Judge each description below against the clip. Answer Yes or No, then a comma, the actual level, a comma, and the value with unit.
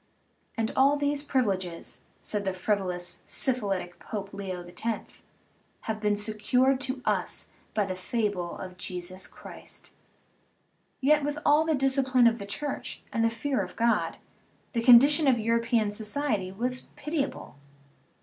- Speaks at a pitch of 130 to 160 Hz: No, high, 230 Hz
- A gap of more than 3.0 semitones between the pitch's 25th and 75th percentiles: Yes, average, 5.2 semitones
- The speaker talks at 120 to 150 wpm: Yes, average, 140 wpm